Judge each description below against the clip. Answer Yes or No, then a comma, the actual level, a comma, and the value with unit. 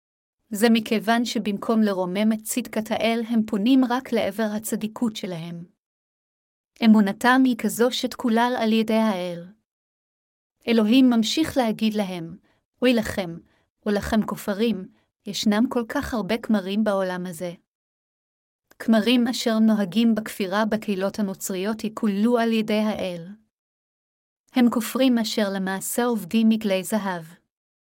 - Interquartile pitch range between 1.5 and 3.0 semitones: Yes, average, 2.7 semitones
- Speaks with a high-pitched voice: Yes, high, 220 Hz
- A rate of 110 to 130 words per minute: Yes, average, 115 wpm